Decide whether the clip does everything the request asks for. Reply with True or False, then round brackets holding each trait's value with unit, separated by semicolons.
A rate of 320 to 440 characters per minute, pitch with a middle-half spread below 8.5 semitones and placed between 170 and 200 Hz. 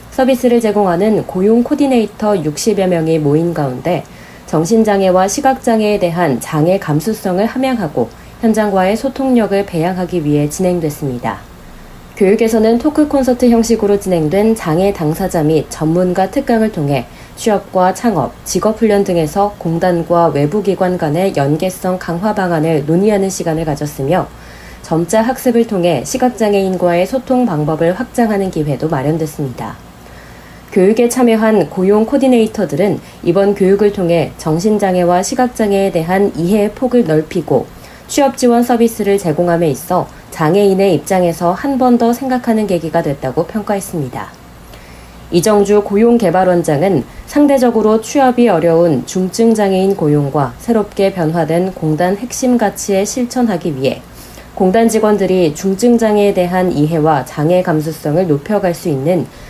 True (330 characters per minute; 5.5 semitones; 185 Hz)